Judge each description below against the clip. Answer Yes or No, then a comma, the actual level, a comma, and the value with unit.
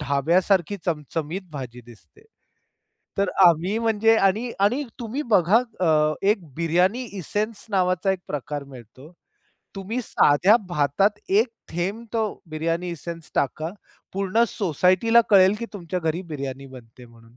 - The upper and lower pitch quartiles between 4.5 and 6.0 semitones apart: Yes, wide, 5.5 semitones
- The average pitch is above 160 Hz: Yes, medium, 180 Hz